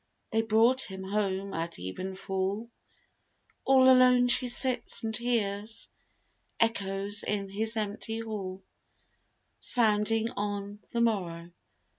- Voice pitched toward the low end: No, high, 210 Hz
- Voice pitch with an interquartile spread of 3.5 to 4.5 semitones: No, average, 2.9 semitones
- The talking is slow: Yes, slow, 110 wpm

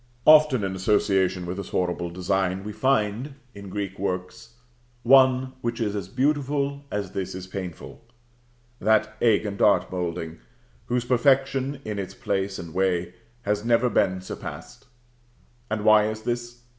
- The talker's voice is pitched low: Yes, low, 105 Hz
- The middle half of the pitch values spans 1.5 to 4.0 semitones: No, average, 4.5 semitones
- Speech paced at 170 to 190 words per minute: No, average, 145 wpm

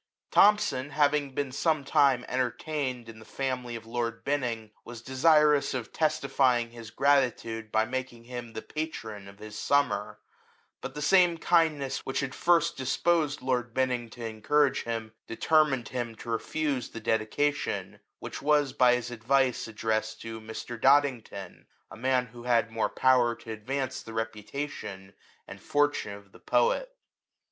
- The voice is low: Yes, low, 125 Hz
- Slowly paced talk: No, average, 155 wpm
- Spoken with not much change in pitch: No, average, 3.9 semitones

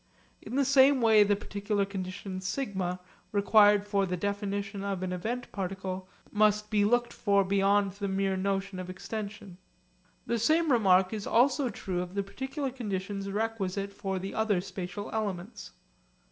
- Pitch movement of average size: No, narrow, 2.3 semitones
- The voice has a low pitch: No, high, 200 Hz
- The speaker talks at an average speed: Yes, average, 155 wpm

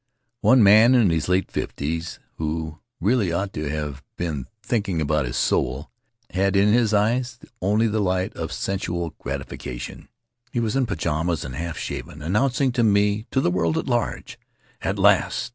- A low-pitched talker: Yes, very low, 95 Hz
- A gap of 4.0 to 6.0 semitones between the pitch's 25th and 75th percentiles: Yes, wide, 5.5 semitones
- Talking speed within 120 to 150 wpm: No, average, 165 wpm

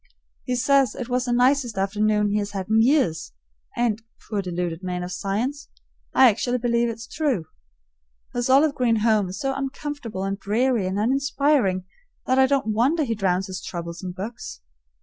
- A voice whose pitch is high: Yes, high, 225 Hz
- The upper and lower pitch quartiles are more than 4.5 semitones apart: Yes, average, 5.1 semitones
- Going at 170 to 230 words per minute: Yes, average, 175 wpm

